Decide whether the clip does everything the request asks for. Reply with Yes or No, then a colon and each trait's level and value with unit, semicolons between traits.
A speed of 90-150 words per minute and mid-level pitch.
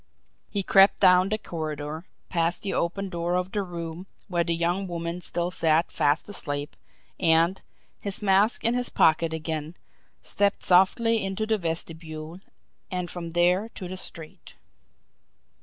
Yes: average, 145 wpm; medium, 175 Hz